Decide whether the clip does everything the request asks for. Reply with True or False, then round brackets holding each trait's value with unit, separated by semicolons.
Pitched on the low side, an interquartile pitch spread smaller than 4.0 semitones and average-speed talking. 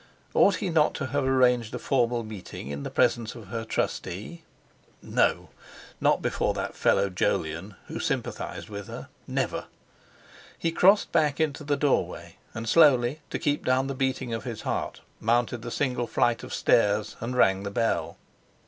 False (120 Hz; 4.4 semitones; 165 wpm)